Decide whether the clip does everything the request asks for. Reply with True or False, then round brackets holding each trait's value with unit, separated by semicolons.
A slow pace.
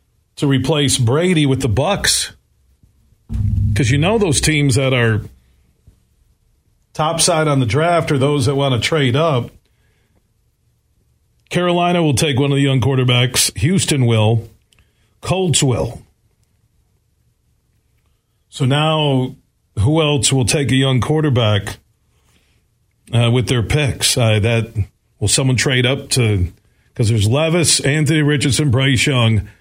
True (130 wpm)